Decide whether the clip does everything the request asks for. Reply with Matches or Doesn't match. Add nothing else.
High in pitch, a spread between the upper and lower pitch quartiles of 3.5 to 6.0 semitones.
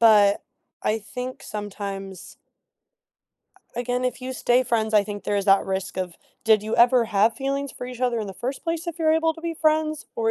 Matches